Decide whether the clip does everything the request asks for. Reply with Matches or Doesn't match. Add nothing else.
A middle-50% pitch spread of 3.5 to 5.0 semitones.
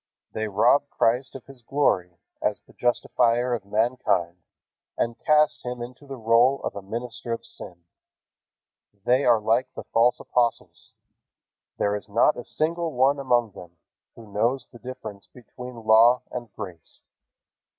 Doesn't match